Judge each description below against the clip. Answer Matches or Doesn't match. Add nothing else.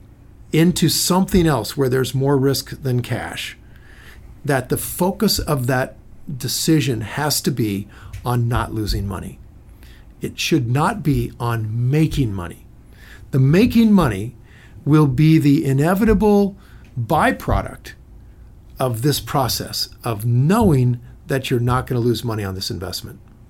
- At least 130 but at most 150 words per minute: Matches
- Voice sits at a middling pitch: Doesn't match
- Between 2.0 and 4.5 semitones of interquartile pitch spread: Doesn't match